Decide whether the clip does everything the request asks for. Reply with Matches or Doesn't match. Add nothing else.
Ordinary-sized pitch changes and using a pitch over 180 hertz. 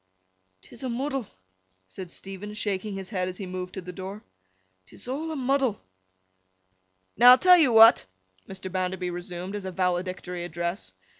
Matches